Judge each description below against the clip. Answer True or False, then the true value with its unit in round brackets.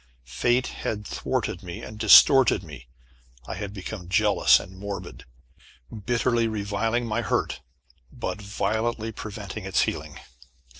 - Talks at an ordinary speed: False (120 wpm)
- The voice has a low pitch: True (105 Hz)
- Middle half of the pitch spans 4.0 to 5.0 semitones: False (2.6 semitones)